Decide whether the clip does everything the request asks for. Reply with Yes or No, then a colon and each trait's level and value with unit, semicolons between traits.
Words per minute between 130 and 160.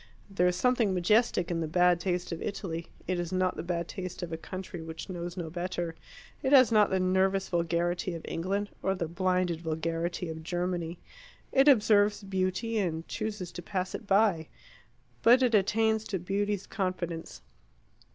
No: average, 170 wpm